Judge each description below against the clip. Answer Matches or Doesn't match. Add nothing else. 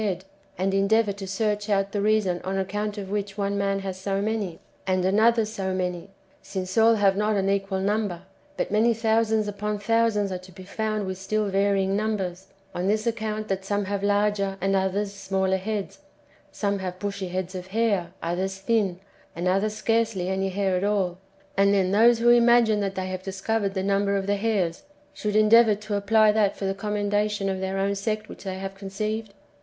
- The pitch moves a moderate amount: Doesn't match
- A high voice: Matches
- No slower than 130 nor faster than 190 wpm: Doesn't match